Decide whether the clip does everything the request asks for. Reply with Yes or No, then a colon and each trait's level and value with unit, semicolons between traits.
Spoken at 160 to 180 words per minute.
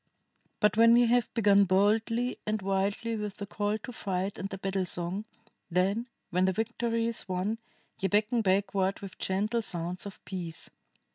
Yes: average, 165 wpm